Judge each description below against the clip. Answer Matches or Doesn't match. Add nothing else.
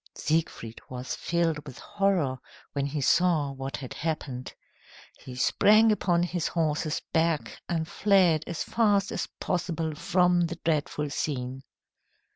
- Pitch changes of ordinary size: Matches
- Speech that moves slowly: Matches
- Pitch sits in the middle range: Matches